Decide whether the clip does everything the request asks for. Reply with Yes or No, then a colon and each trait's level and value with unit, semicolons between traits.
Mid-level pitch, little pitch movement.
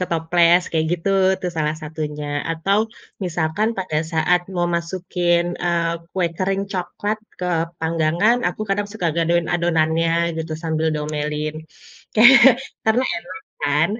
Yes: medium, 170 Hz; narrow, 2.3 semitones